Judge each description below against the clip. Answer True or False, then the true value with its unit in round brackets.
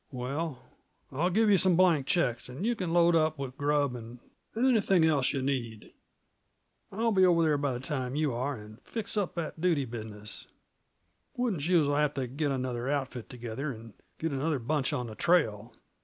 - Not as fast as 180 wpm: False (185 wpm)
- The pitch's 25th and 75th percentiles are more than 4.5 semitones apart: True (5.3 semitones)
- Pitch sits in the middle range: True (145 Hz)